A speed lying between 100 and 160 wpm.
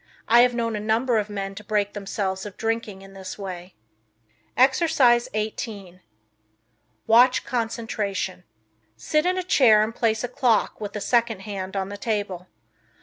Yes: average, 155 wpm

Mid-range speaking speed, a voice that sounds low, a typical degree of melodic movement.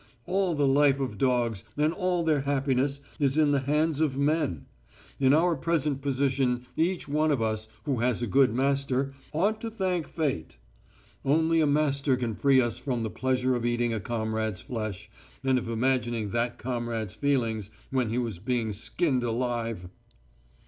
Yes: average, 170 wpm; low, 130 Hz; average, 3.7 semitones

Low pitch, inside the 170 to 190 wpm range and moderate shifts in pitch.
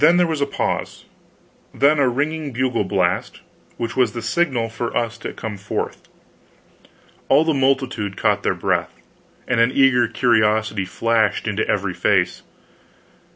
No: low, 120 Hz; average, 145 wpm; average, 3.9 semitones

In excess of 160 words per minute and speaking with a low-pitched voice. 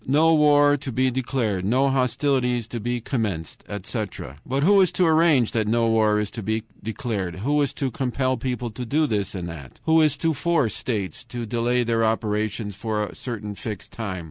Yes: average, 195 wpm; low, 120 Hz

